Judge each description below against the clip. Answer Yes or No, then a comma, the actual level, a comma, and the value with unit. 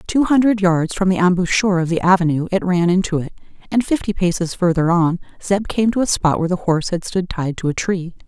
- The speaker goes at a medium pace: No, fast, 230 wpm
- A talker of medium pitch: Yes, medium, 180 Hz